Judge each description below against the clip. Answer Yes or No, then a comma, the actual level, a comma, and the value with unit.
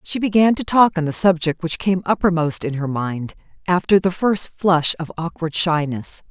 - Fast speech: No, average, 190 wpm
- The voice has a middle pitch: Yes, medium, 170 Hz